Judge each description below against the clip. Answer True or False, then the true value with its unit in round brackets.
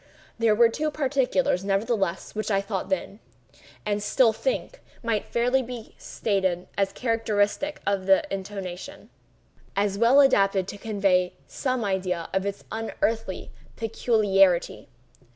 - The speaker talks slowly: True (120 wpm)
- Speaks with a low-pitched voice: False (210 Hz)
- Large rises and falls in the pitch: False (3.3 semitones)